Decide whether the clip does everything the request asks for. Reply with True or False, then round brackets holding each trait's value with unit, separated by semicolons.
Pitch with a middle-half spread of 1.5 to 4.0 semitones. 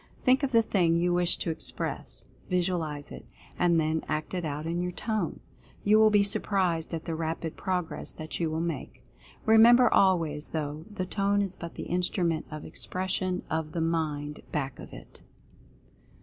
True (3.1 semitones)